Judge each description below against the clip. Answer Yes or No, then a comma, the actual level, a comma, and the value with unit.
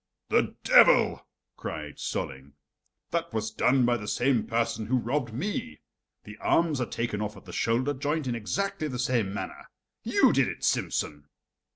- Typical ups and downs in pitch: Yes, average, 4.2 semitones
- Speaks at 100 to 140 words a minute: No, average, 165 wpm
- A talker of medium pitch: No, low, 120 Hz